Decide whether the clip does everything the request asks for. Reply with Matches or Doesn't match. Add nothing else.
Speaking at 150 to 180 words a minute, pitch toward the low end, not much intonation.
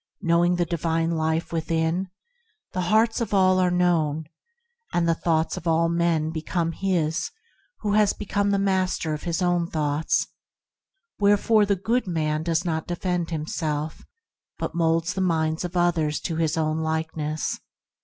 Doesn't match